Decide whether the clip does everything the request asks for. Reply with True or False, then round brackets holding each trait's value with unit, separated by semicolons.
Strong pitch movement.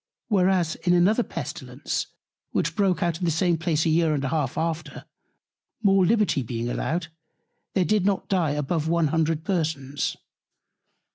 False (3.1 semitones)